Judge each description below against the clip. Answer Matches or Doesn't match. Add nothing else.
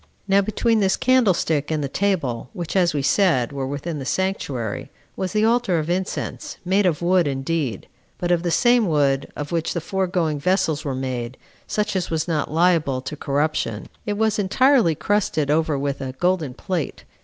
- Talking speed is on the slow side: Doesn't match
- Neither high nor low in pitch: Matches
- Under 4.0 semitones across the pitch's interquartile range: Doesn't match